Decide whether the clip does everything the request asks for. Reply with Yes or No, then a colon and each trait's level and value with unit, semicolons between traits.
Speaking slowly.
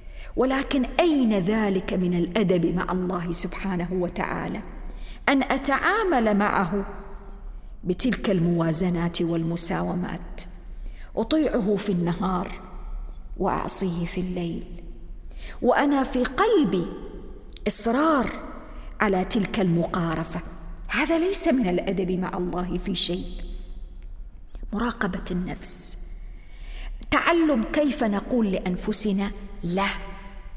Yes: slow, 85 wpm